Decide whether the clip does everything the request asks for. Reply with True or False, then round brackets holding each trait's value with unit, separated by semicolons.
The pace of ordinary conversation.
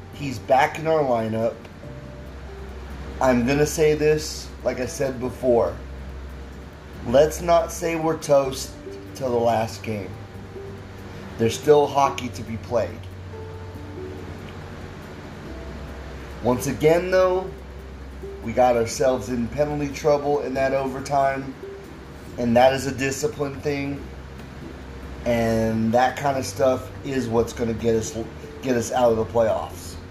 False (130 wpm)